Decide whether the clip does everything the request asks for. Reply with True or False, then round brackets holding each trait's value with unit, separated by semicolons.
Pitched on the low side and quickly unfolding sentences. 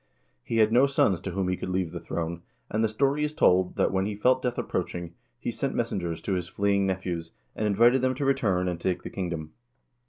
True (95 Hz; 225 wpm)